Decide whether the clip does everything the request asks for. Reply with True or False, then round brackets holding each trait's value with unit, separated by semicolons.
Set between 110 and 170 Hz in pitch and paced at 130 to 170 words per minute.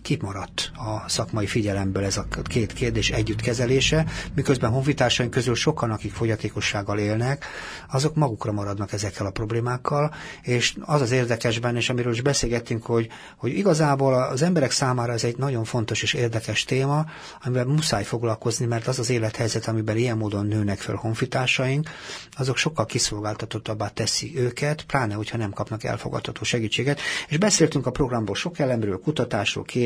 True (120 Hz; 150 wpm)